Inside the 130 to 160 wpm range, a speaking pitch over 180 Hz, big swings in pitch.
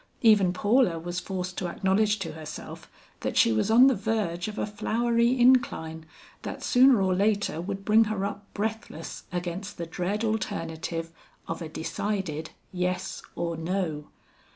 No: average, 155 wpm; high, 190 Hz; average, 4.3 semitones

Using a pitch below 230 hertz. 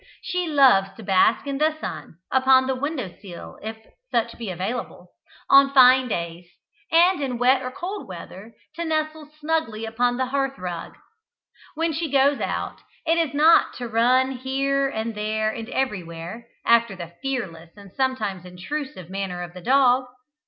No: very high, 250 Hz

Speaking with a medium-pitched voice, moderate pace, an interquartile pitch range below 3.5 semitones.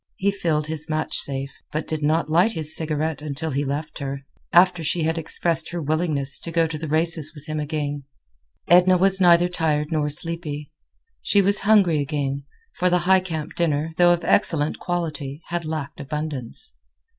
Yes: medium, 155 Hz; average, 175 wpm; average, 2.7 semitones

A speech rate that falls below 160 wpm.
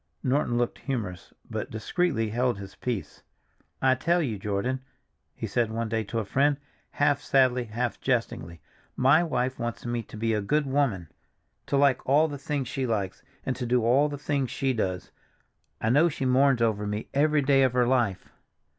No: average, 185 wpm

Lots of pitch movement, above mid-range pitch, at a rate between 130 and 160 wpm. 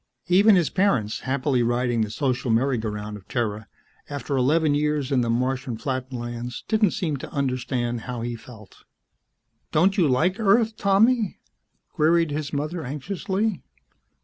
No: wide, 6.1 semitones; low, 135 Hz; average, 150 wpm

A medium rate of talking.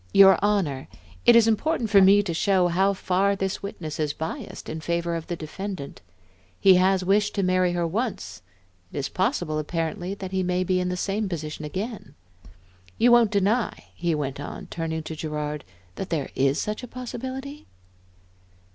Yes: average, 180 wpm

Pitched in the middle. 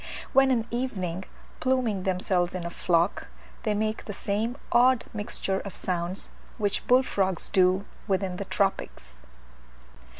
No: high, 200 Hz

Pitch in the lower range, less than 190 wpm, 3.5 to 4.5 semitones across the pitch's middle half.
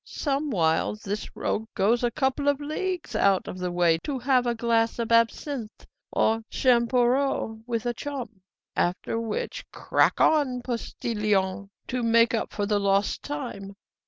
No: high, 230 Hz; average, 150 wpm; average, 3.9 semitones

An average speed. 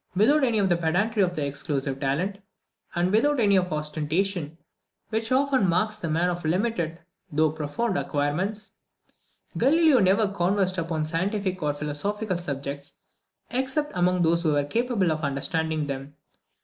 Yes: average, 150 wpm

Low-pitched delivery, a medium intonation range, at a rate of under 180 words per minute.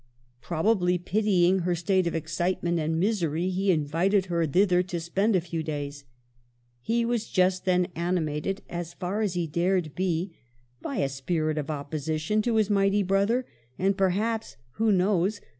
No: medium, 180 Hz; average, 3.4 semitones; average, 160 wpm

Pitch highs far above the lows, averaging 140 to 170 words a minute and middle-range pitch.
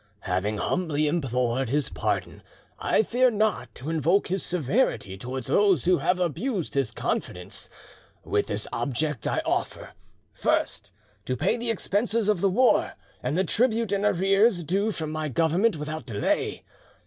Yes: wide, 7.3 semitones; average, 150 wpm; medium, 170 Hz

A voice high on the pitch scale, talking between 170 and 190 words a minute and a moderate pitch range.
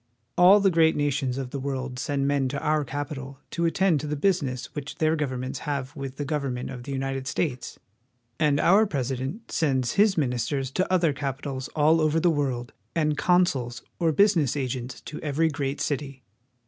No: medium, 145 Hz; average, 185 wpm; average, 3.2 semitones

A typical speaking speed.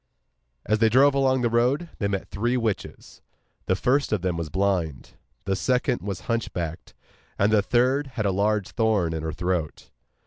Yes: average, 175 wpm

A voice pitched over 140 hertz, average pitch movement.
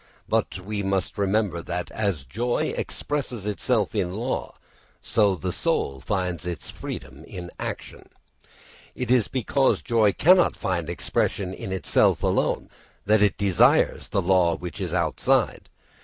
No: very low, 95 Hz; average, 3.6 semitones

